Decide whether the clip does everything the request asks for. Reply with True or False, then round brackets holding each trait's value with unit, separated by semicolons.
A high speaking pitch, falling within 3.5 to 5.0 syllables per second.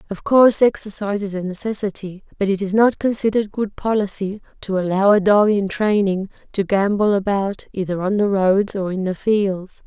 False (200 Hz; 5.2 syllables/s)